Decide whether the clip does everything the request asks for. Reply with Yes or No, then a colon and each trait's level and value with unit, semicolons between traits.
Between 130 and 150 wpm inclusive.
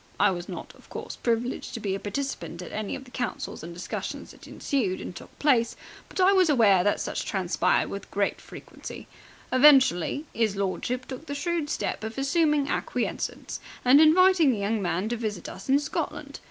No: average, 185 wpm